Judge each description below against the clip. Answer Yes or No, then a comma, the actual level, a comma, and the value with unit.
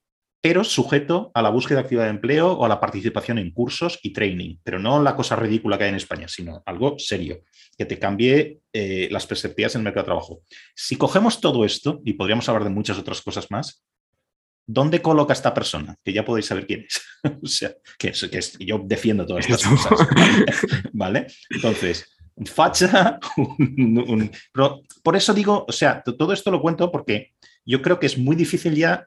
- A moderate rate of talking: No, fast, 200 wpm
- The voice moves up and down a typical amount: No, wide, 6.2 semitones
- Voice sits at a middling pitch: No, low, 130 Hz